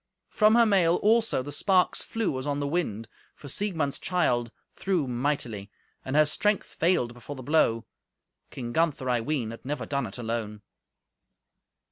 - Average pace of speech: Yes, average, 160 wpm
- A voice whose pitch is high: No, medium, 145 Hz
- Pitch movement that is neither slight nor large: No, wide, 6.6 semitones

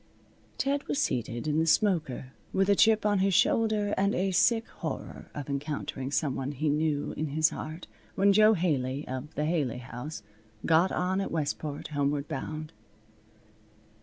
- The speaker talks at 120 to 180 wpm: Yes, average, 165 wpm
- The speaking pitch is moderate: Yes, medium, 155 Hz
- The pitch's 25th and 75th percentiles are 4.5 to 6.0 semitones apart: Yes, wide, 5.4 semitones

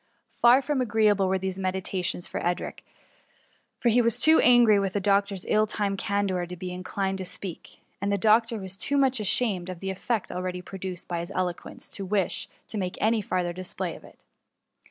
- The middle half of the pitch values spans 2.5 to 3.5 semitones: Yes, average, 2.9 semitones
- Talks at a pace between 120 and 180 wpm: No, average, 190 wpm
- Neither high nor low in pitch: No, high, 195 Hz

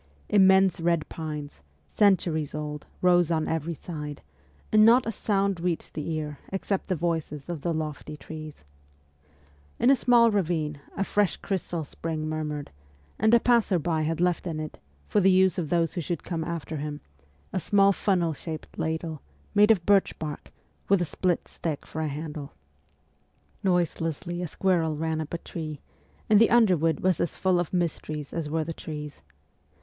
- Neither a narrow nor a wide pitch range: Yes, average, 3.4 semitones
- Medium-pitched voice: Yes, medium, 165 Hz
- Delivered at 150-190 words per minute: Yes, average, 170 wpm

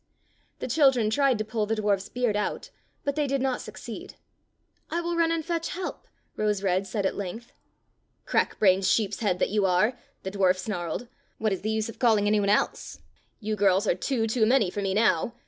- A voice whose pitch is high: Yes, high, 215 Hz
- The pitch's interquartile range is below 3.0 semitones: No, average, 4.1 semitones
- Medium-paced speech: No, fast, 215 wpm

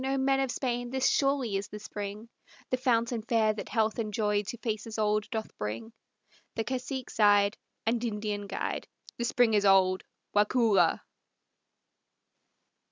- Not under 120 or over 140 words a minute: No, average, 150 wpm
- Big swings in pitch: No, average, 2.9 semitones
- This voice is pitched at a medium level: No, high, 220 Hz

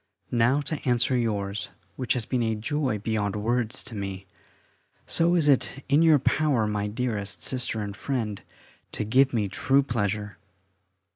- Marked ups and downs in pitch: No, average, 4.3 semitones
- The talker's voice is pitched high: No, low, 115 Hz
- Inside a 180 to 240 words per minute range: No, average, 155 wpm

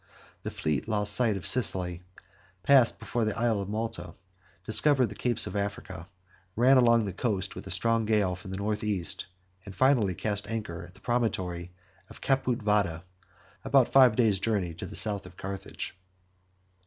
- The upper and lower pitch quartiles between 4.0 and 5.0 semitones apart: No, average, 3.6 semitones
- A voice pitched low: Yes, low, 105 Hz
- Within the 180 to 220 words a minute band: No, average, 170 wpm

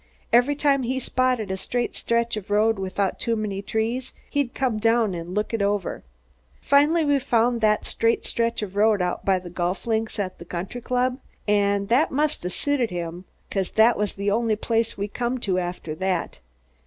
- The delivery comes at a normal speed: Yes, average, 190 wpm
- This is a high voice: Yes, high, 220 Hz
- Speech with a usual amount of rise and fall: Yes, average, 3.8 semitones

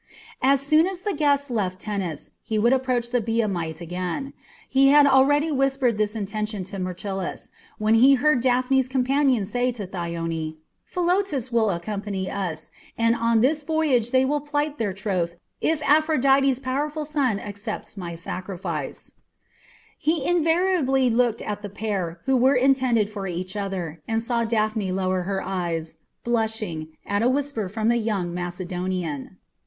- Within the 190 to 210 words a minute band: No, average, 150 wpm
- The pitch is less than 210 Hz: No, high, 225 Hz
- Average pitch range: No, wide, 6.1 semitones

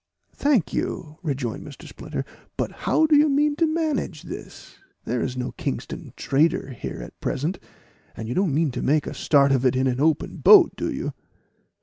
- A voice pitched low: No, medium, 150 Hz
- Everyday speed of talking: Yes, average, 190 wpm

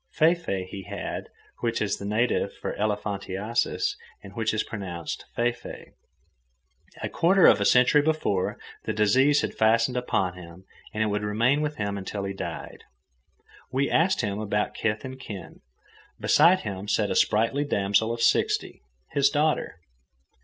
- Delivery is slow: No, average, 160 wpm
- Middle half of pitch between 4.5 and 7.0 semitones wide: Yes, average, 4.9 semitones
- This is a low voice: Yes, low, 110 Hz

